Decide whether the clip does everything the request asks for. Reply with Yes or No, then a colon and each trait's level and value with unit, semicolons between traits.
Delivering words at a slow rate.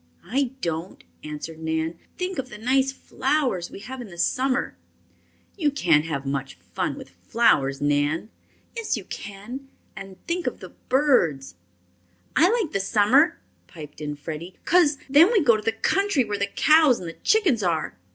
No: average, 170 wpm